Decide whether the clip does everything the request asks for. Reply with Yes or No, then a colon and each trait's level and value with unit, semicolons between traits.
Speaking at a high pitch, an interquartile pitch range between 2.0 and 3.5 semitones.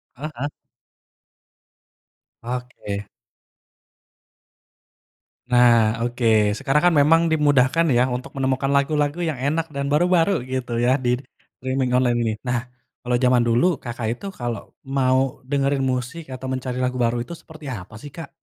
No: low, 130 Hz; average, 2.9 semitones